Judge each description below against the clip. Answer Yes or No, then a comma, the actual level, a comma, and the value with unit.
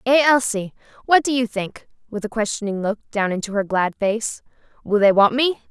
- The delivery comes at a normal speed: Yes, average, 190 wpm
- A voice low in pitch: No, high, 220 Hz